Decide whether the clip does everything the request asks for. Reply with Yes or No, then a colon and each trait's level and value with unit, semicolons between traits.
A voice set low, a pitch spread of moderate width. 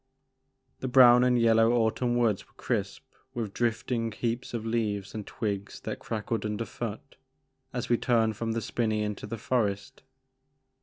No: low, 115 Hz; narrow, 2.1 semitones